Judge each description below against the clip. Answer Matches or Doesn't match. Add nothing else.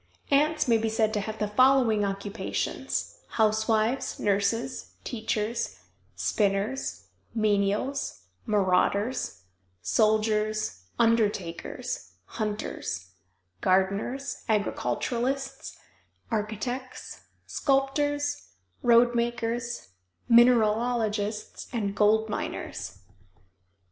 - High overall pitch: Matches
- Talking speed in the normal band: Doesn't match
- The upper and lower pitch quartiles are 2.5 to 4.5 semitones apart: Matches